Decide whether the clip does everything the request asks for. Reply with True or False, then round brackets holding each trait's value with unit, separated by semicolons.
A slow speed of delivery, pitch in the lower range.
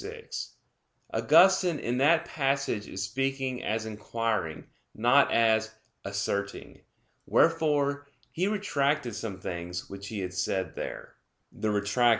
True (115 wpm; 115 Hz)